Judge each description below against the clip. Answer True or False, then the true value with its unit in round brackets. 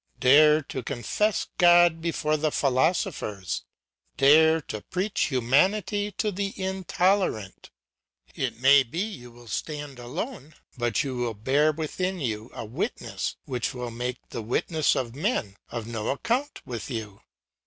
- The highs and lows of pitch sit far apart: True (6.5 semitones)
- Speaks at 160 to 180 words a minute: False (140 wpm)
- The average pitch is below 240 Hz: True (140 Hz)